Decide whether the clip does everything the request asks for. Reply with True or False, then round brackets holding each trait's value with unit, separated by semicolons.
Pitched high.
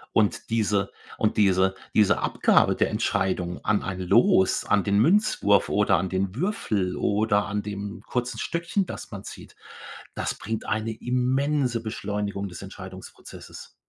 False (105 Hz)